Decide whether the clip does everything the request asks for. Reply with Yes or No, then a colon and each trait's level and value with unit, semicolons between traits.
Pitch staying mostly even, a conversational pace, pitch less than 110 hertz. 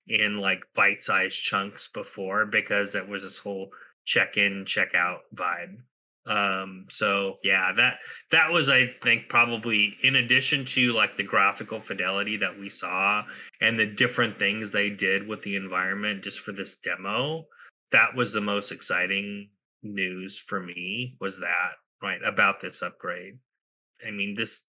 Yes: narrow, 2.0 semitones; average, 160 wpm; low, 100 Hz